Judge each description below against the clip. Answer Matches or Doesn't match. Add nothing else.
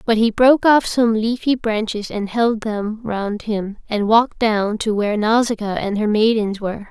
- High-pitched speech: Matches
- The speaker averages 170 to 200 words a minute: Matches